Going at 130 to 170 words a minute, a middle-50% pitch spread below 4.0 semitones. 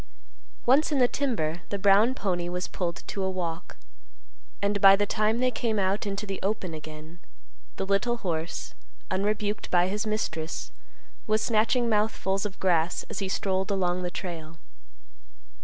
Yes: average, 155 wpm; average, 3.3 semitones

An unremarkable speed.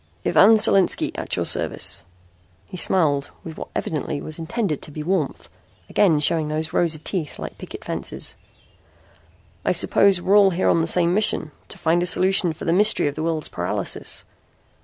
Yes: average, 180 wpm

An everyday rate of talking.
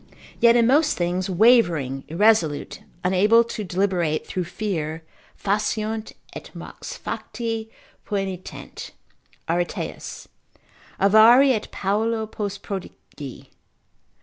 No: slow, 95 wpm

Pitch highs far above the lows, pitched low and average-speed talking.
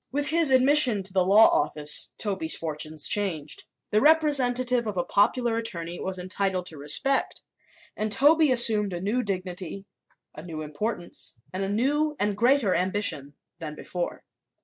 No: wide, 6.2 semitones; high, 200 Hz; average, 150 wpm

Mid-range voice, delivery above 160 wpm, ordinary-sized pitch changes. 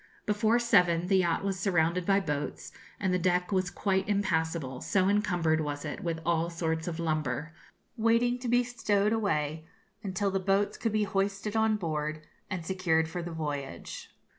Yes: medium, 180 Hz; average, 170 wpm; average, 4.0 semitones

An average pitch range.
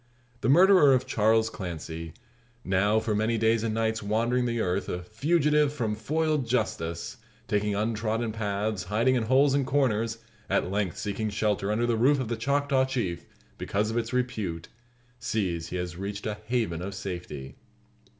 Yes: average, 3.9 semitones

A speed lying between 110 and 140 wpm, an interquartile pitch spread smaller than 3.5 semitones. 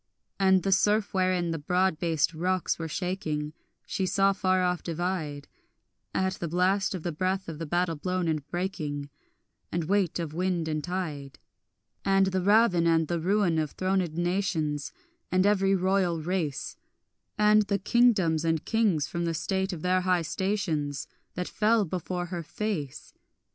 No: average, 160 wpm; average, 2.8 semitones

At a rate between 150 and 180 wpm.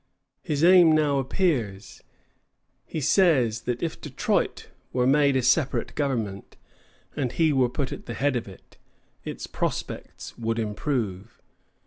No: slow, 135 wpm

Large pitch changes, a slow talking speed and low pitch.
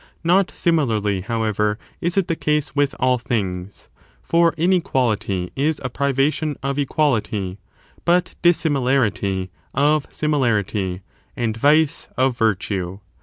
Yes: wide, 6.5 semitones; slow, 115 wpm; low, 130 Hz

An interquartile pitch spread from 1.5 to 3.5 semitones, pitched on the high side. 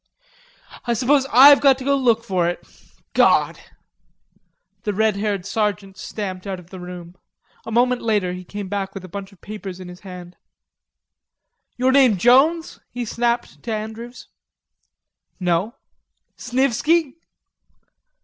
No: average, 4.8 semitones; high, 215 Hz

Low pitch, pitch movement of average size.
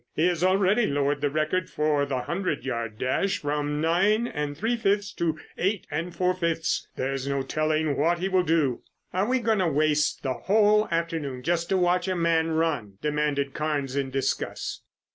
No: medium, 160 Hz; average, 4.2 semitones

